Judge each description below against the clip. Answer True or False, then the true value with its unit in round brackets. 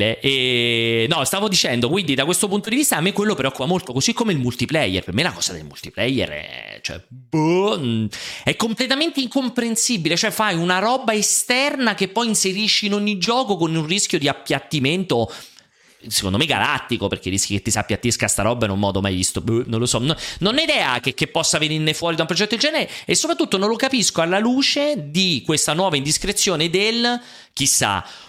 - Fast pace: True (205 wpm)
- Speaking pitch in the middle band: True (170 Hz)